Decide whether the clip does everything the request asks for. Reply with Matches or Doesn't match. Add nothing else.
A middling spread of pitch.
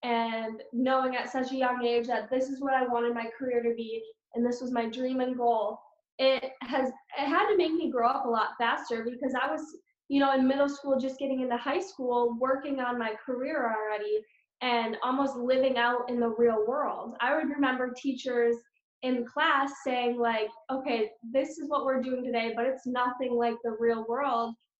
Doesn't match